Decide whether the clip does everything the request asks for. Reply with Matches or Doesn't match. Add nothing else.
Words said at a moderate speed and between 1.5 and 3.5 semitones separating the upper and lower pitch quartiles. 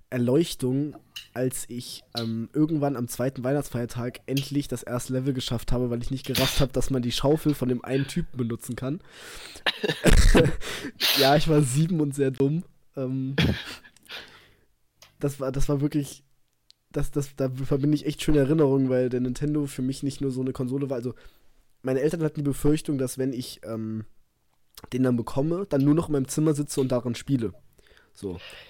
Matches